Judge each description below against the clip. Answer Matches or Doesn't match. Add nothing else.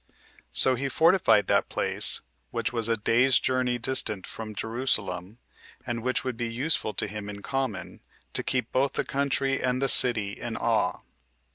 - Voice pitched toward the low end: Matches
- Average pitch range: Matches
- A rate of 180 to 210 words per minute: Doesn't match